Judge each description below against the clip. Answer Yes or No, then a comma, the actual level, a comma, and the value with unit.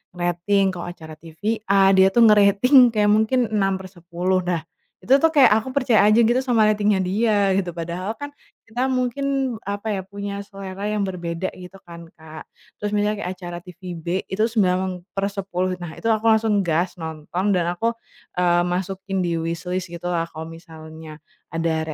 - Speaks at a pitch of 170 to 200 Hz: Yes, high, 190 Hz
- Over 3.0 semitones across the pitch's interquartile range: Yes, average, 3.5 semitones